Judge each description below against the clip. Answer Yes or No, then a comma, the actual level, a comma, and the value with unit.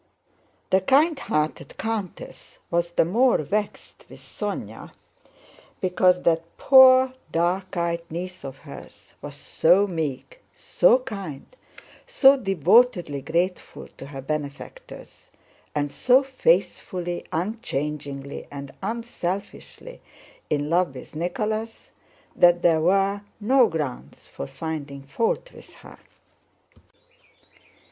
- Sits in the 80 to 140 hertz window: No, medium, 180 Hz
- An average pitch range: No, wide, 6.5 semitones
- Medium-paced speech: No, slow, 105 wpm